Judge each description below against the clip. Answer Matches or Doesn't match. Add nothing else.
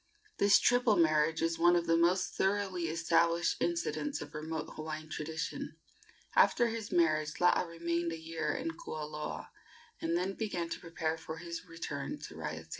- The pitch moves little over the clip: Matches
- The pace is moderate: Matches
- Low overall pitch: Doesn't match